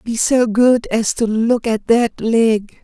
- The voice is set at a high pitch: Yes, high, 225 Hz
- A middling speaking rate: Yes, average, 190 wpm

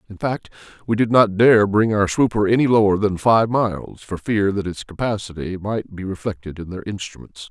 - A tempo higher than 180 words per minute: Yes, average, 200 wpm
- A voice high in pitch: No, low, 105 Hz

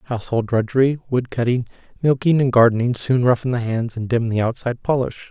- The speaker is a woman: No, male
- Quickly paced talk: No, average, 170 wpm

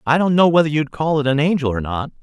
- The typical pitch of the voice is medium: Yes, medium, 145 Hz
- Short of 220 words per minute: No, fast, 295 wpm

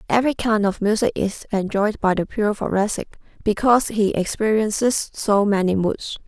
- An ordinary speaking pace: Yes, average, 155 wpm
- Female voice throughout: Yes, female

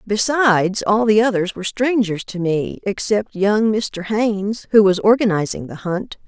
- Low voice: No, high, 205 Hz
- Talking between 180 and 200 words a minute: No, average, 160 wpm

